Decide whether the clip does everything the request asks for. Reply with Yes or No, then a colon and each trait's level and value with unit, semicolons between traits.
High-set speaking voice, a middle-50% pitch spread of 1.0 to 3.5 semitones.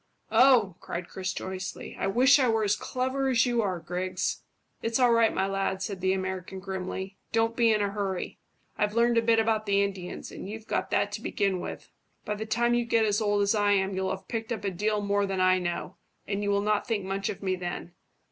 Yes: high, 205 Hz; average, 2.9 semitones